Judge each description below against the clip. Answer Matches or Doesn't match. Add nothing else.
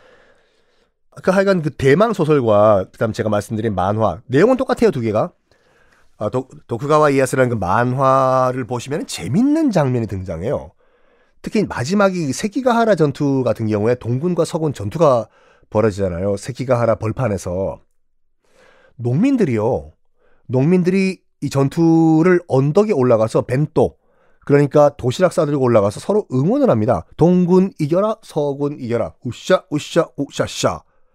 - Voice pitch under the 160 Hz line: Matches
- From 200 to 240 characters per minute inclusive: Doesn't match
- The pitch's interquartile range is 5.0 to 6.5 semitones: Doesn't match